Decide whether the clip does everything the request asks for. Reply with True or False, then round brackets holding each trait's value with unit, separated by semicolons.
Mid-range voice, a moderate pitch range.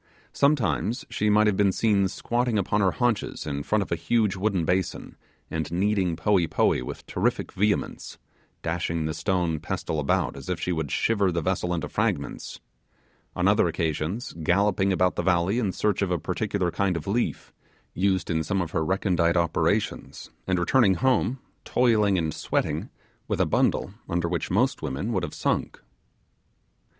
False (95 Hz; 3.7 semitones)